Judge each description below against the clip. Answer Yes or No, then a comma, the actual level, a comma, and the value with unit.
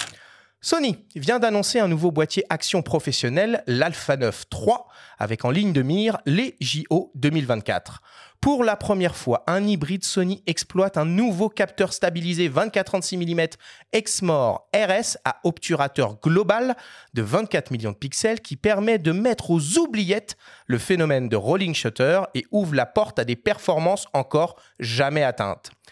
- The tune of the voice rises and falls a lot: Yes, wide, 5.7 semitones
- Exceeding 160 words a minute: No, average, 150 wpm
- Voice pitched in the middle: Yes, medium, 175 Hz